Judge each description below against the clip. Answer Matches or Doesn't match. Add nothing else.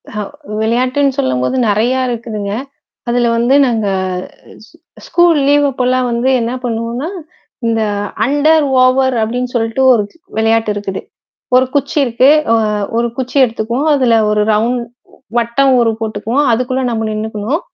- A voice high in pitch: Matches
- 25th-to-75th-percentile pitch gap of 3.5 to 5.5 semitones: Doesn't match